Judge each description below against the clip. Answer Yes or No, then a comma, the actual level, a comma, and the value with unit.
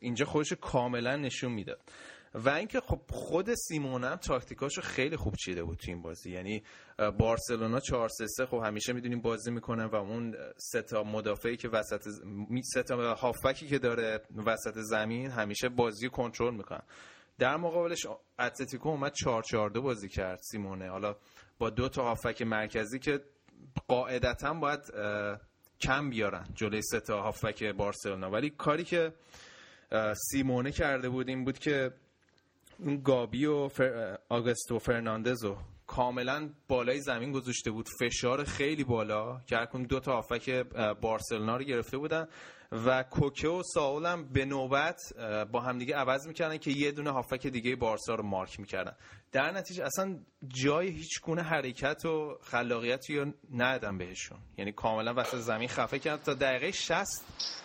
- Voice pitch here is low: Yes, low, 125 Hz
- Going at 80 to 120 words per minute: No, average, 150 wpm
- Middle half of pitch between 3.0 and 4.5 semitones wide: Yes, average, 4.0 semitones